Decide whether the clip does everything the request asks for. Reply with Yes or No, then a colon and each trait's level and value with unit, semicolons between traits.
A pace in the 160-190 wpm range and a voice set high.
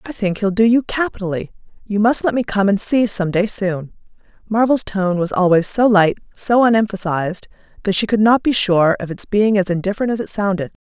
No: fast, 205 wpm; high, 205 Hz